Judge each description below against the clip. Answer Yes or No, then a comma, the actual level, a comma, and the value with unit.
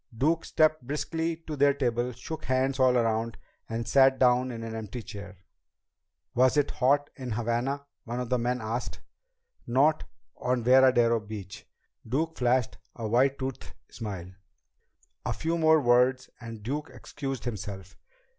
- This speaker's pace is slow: No, average, 145 wpm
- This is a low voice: Yes, low, 125 Hz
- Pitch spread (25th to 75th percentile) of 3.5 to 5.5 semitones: No, average, 3.1 semitones